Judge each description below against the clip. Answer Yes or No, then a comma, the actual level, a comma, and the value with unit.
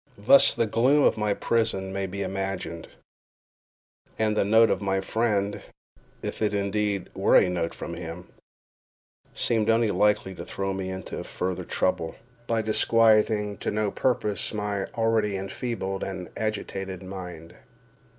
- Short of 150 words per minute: Yes, average, 140 wpm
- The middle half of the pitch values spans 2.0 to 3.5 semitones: Yes, narrow, 2.4 semitones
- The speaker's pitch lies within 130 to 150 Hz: No, low, 100 Hz